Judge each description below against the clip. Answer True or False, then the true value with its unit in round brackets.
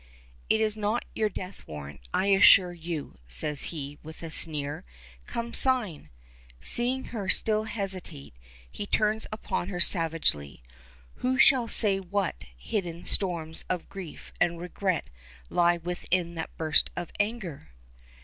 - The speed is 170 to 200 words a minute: False (135 wpm)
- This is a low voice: False (180 Hz)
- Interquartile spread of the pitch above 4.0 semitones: True (4.7 semitones)